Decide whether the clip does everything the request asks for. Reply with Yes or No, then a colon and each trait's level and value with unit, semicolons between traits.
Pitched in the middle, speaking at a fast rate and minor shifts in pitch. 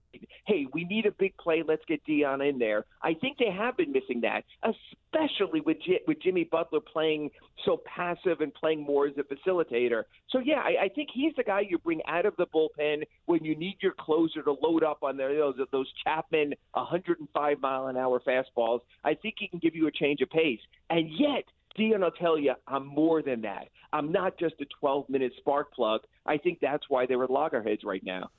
No: medium, 155 Hz; fast, 215 wpm; average, 5.0 semitones